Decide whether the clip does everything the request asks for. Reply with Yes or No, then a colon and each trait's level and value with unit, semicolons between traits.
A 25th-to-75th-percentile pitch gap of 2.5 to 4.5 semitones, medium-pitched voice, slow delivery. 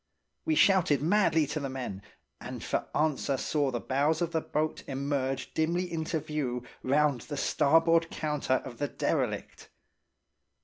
No: average, 3.1 semitones; medium, 150 Hz; average, 145 wpm